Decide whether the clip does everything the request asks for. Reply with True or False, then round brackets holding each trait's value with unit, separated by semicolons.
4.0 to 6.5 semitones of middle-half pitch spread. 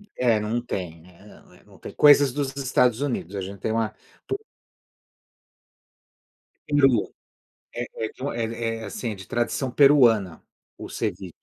True (4.6 semitones)